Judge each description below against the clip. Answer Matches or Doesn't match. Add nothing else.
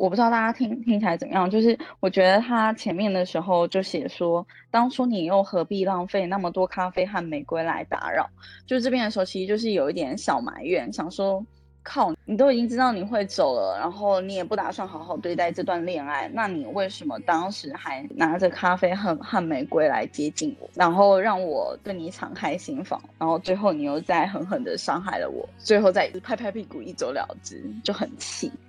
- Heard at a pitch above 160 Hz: Matches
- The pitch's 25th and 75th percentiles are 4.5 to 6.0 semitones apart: Doesn't match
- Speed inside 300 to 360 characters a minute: Matches